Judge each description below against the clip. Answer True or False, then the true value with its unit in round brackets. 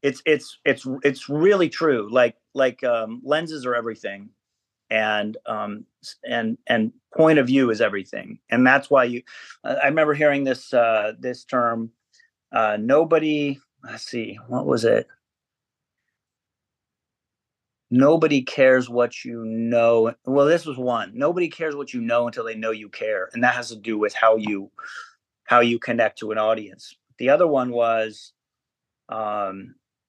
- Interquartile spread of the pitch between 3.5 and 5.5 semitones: True (4.7 semitones)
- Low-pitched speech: True (125 Hz)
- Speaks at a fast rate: False (155 wpm)